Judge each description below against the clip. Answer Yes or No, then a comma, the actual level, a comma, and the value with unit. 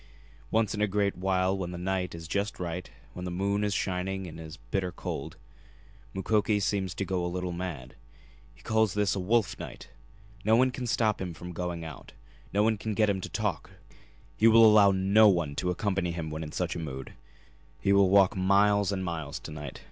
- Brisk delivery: Yes, fast, 210 wpm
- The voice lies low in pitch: Yes, very low, 95 Hz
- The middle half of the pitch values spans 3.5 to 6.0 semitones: No, average, 2.8 semitones